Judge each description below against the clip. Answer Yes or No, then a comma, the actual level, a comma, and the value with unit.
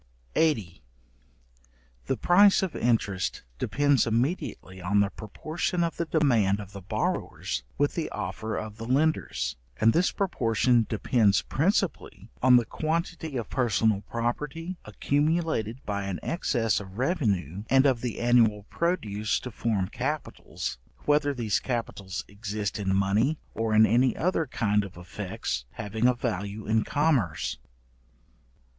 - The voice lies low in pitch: Yes, low, 115 Hz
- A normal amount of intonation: No, wide, 6.0 semitones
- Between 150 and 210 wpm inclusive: No, slow, 135 wpm